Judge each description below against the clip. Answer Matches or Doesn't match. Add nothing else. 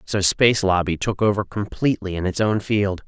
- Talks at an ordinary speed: Matches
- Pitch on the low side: Matches